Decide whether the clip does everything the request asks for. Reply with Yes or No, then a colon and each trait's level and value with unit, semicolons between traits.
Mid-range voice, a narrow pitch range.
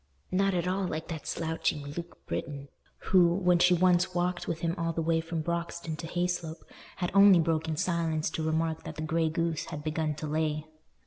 Yes: medium, 165 Hz; narrow, 1.8 semitones